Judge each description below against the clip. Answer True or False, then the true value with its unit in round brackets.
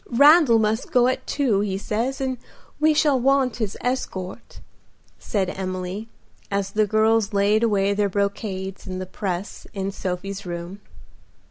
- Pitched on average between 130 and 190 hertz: False (205 Hz)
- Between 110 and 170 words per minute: True (145 wpm)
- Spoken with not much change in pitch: False (3.8 semitones)